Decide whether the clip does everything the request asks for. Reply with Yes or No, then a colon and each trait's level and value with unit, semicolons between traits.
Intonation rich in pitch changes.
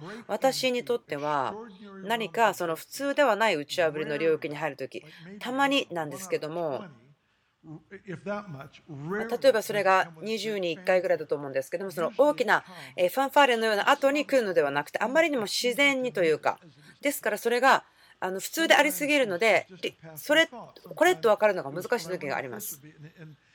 Yes: wide, 7.8 semitones